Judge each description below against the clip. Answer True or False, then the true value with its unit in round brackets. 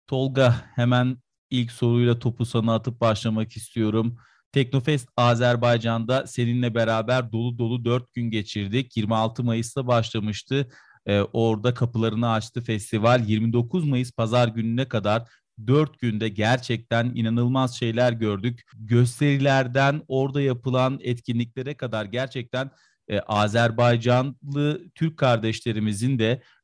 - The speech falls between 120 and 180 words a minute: False (110 wpm)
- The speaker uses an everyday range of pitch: False (2.3 semitones)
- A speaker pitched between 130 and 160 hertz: False (120 Hz)